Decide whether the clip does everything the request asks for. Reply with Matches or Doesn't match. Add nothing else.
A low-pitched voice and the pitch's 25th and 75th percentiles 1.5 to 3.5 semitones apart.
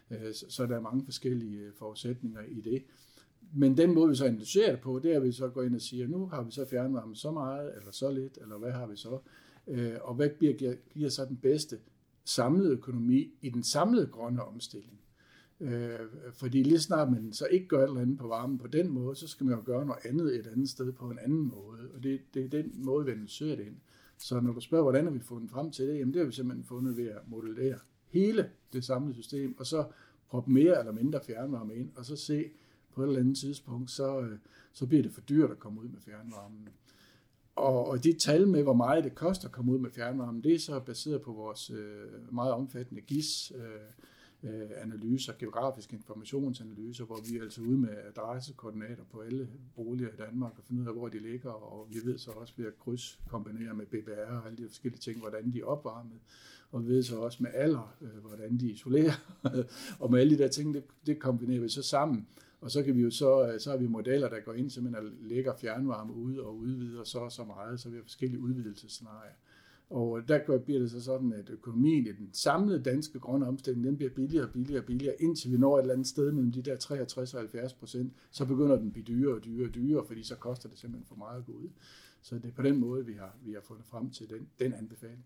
Matches